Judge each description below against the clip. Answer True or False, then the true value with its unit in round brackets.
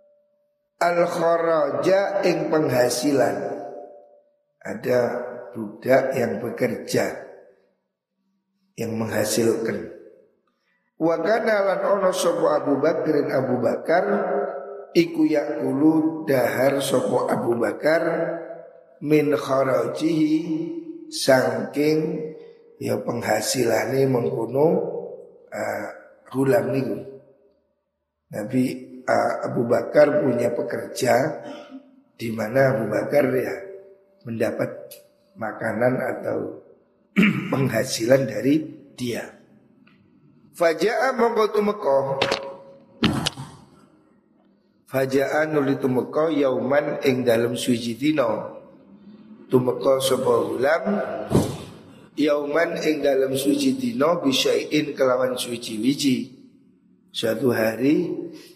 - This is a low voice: False (155 Hz)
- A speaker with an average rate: False (80 wpm)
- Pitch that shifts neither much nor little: False (7.9 semitones)